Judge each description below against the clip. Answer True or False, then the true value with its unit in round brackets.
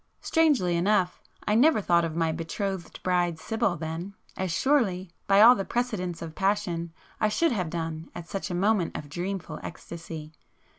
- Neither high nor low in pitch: True (180 Hz)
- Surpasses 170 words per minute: False (165 wpm)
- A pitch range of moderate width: True (3.9 semitones)